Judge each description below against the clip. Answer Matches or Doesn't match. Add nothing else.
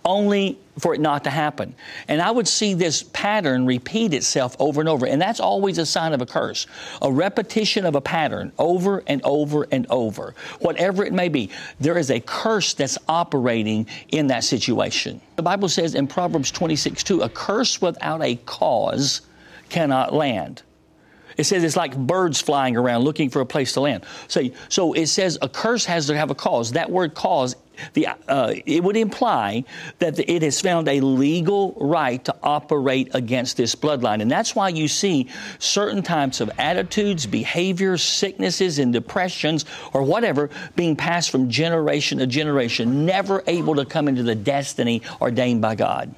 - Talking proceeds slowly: Doesn't match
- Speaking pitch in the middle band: Matches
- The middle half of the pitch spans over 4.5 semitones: Matches